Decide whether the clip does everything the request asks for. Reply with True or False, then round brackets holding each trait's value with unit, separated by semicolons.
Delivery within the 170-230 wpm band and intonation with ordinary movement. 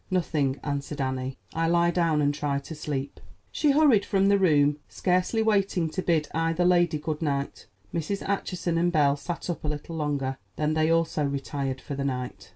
True (185 wpm; 3.7 semitones)